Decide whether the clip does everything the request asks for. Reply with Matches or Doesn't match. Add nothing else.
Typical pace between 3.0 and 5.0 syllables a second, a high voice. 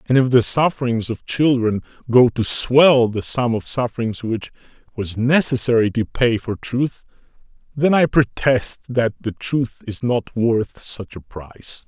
Doesn't match